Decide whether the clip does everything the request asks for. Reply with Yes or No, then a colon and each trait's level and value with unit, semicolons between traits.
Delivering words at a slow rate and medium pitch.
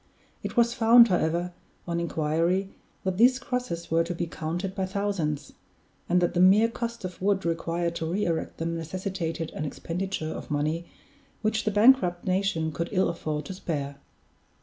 No: average, 170 wpm; medium, 175 Hz